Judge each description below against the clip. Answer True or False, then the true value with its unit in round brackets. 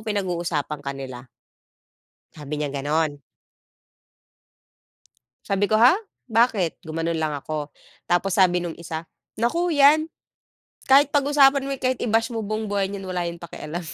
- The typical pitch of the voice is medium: True (180 Hz)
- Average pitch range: False (6.7 semitones)